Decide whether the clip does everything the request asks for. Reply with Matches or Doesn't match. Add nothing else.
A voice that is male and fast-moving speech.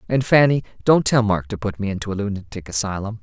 Matches